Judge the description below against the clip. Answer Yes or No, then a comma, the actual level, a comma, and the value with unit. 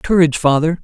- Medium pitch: Yes, medium, 160 Hz